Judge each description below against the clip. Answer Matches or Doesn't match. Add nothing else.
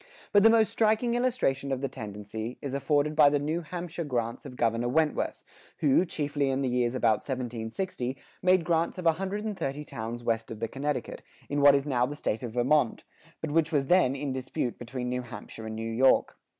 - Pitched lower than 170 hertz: Matches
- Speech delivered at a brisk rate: Matches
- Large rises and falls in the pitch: Doesn't match